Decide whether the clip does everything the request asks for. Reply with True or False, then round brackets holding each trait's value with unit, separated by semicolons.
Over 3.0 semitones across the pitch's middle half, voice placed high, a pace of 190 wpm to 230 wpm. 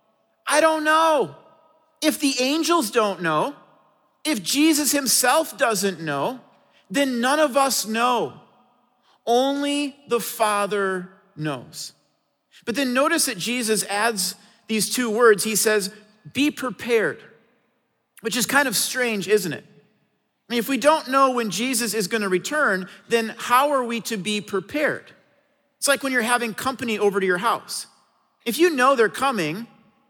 False (4.7 semitones; 245 Hz; 150 wpm)